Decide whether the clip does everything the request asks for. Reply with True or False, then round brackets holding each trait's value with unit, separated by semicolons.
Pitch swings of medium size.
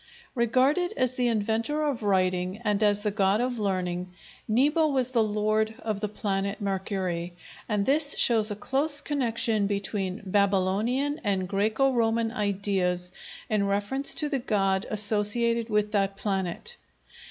True (3.6 semitones)